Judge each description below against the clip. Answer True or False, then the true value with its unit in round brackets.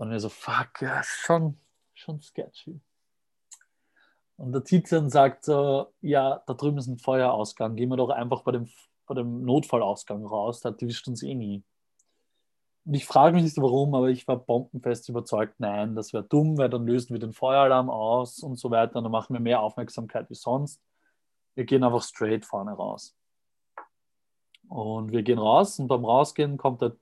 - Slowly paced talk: False (180 wpm)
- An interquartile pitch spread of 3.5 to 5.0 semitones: False (2.9 semitones)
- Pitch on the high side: False (125 Hz)